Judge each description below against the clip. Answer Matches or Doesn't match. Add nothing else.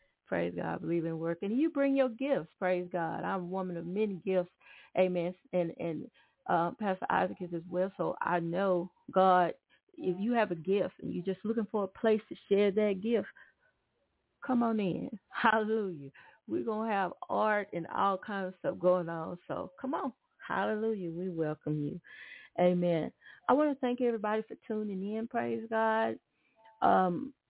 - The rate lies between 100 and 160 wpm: Doesn't match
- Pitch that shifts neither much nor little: Matches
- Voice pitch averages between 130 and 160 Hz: Doesn't match